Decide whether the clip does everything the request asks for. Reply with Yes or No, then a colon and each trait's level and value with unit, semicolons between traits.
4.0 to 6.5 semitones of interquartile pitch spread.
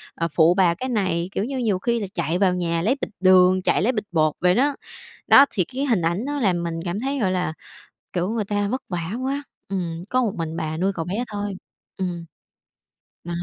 Yes: average, 4.6 semitones